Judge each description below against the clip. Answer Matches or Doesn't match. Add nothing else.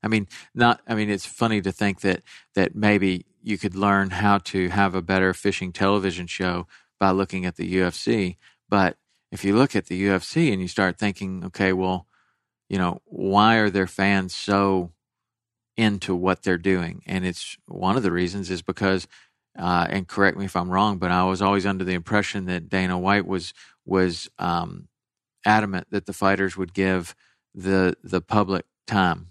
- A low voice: Matches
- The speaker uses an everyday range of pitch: Doesn't match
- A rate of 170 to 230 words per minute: Matches